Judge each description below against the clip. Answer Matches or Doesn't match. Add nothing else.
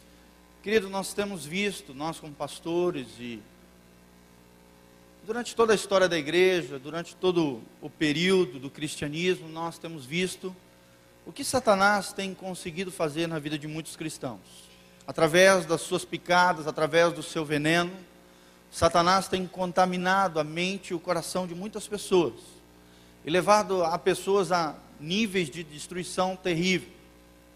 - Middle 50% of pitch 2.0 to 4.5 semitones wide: Doesn't match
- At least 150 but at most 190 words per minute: Doesn't match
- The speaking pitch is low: Doesn't match